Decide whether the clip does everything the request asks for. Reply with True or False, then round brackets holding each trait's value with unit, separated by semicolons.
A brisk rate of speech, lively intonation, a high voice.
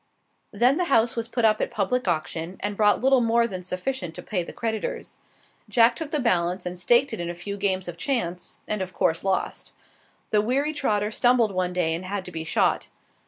False (215 wpm; 4.8 semitones; 205 Hz)